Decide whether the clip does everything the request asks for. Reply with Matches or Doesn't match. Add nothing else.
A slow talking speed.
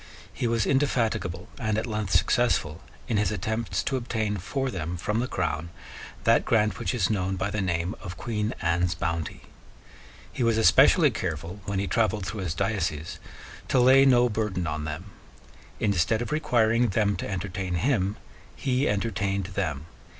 Doesn't match